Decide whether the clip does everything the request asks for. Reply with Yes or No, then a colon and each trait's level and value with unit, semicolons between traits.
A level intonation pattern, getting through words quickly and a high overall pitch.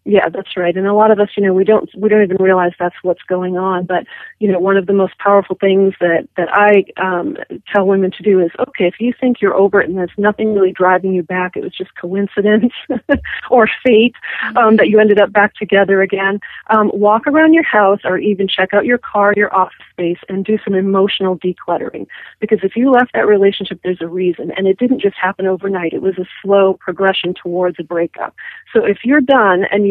Yes: narrow, 2.2 semitones; fast, 230 wpm; high, 195 Hz